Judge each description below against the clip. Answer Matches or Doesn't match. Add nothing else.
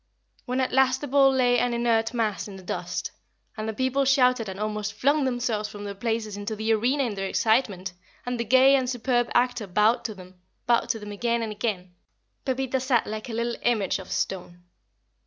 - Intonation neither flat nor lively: Matches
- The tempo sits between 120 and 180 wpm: Doesn't match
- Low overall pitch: Doesn't match